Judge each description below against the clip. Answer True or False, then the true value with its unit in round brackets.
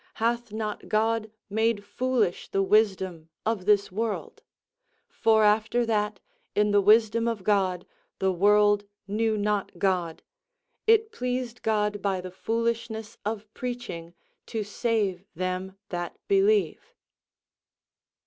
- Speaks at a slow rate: True (120 wpm)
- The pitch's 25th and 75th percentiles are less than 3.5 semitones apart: True (2.7 semitones)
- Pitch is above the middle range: True (210 Hz)